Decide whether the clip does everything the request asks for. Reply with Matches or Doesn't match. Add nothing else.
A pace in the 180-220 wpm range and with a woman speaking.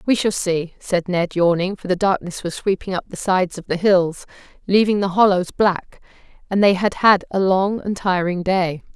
Matches